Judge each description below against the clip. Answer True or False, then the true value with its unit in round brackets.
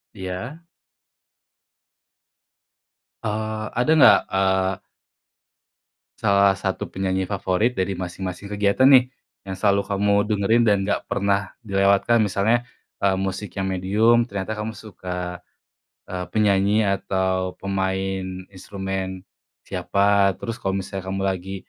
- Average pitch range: False (1.8 semitones)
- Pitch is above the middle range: False (100 Hz)